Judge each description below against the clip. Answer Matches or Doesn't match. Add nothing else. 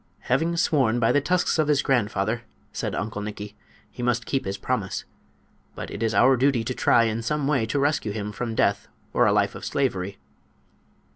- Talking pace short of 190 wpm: Doesn't match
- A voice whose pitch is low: Matches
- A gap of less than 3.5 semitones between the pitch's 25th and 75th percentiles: Doesn't match